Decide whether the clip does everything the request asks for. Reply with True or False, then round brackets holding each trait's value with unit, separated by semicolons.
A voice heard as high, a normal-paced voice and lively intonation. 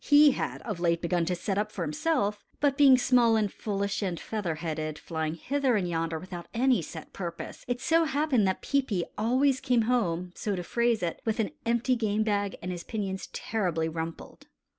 True (205 Hz; 195 wpm; 6.1 semitones)